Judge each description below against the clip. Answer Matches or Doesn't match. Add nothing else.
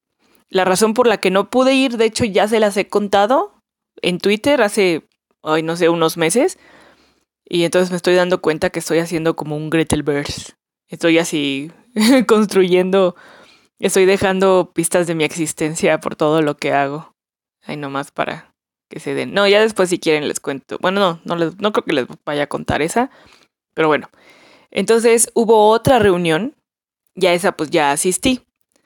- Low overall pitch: Doesn't match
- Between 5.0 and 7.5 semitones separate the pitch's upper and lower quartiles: Doesn't match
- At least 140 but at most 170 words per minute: Doesn't match